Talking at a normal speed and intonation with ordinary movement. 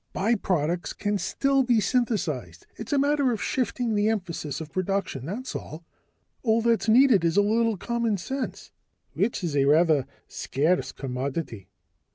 No: average, 150 wpm; wide, 6.6 semitones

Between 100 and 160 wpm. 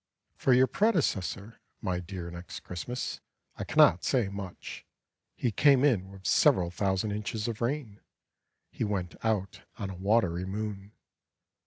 Yes: average, 140 wpm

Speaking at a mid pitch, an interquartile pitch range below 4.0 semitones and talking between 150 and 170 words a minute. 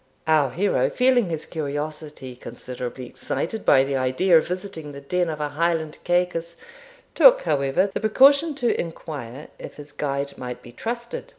No: medium, 155 Hz; average, 4.9 semitones; average, 160 wpm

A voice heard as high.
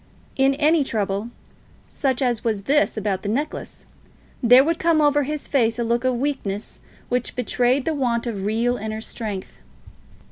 Yes: high, 245 Hz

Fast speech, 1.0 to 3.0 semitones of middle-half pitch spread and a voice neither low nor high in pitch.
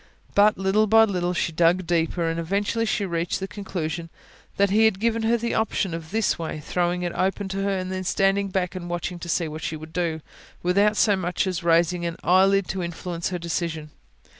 Yes: fast, 215 wpm; average, 2.7 semitones; medium, 180 Hz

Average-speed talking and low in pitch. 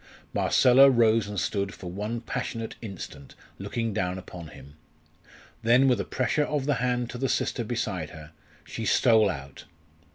Yes: average, 160 wpm; low, 115 Hz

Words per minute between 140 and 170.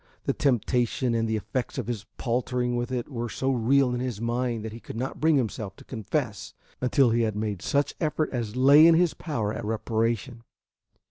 No: average, 200 wpm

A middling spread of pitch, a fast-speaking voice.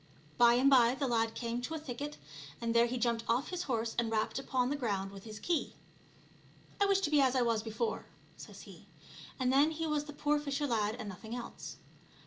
Yes: average, 4.1 semitones; fast, 230 wpm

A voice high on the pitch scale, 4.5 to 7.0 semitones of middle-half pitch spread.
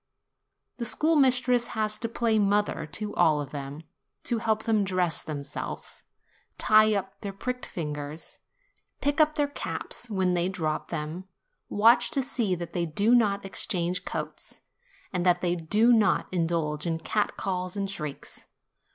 Yes: high, 195 Hz; average, 4.9 semitones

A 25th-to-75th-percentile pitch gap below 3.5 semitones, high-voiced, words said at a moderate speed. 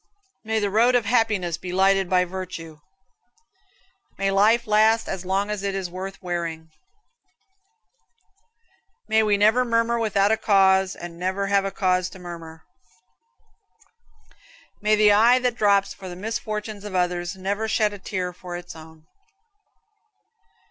Yes: average, 2.9 semitones; high, 195 Hz; average, 145 wpm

